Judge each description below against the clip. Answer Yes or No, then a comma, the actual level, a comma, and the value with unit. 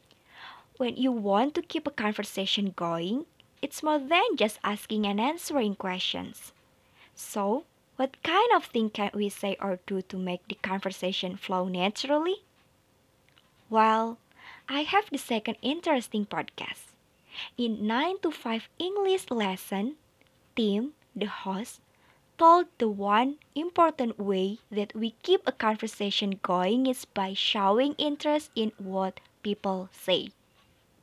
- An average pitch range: No, wide, 6.4 semitones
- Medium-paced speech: No, slow, 130 wpm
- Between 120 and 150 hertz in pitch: No, high, 225 Hz